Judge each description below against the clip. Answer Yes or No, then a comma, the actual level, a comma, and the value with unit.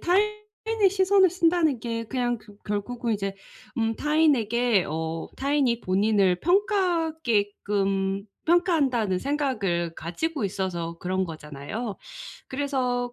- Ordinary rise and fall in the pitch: No, wide, 8.5 semitones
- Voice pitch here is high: Yes, high, 240 Hz